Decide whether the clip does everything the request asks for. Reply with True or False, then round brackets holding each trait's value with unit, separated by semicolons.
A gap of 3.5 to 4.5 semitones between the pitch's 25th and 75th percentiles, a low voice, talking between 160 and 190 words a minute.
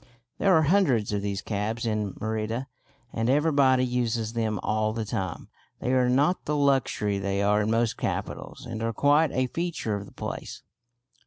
True (3.9 semitones; 115 Hz; 175 wpm)